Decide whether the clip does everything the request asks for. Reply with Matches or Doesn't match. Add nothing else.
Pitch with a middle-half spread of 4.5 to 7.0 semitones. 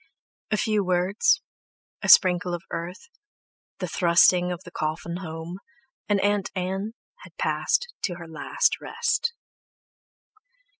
Doesn't match